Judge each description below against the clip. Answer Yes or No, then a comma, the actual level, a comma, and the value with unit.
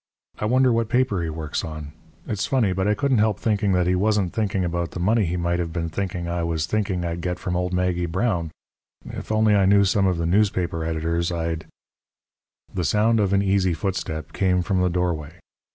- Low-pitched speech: Yes, very low, 90 Hz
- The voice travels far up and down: No, average, 3.2 semitones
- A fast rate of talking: Yes, fast, 215 wpm